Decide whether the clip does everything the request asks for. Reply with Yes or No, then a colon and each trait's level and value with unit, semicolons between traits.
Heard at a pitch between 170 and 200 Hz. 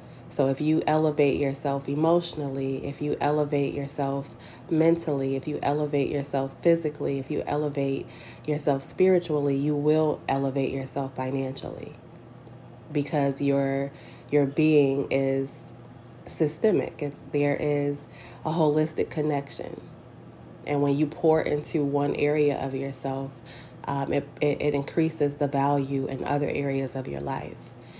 No: medium, 140 Hz